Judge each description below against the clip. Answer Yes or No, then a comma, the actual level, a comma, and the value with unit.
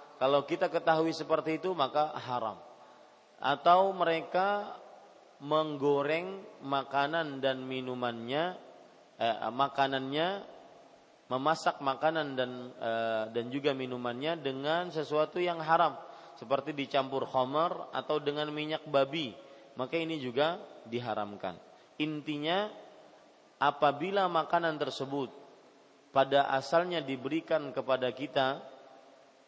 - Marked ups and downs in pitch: No, average, 3.4 semitones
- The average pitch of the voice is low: No, medium, 145 Hz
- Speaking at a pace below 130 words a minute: Yes, average, 95 wpm